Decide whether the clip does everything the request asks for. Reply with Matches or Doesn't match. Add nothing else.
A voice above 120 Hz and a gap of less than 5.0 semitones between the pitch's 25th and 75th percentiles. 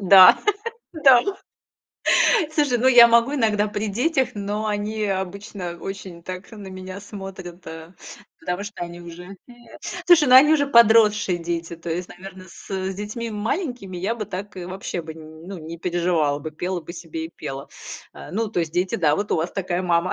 Matches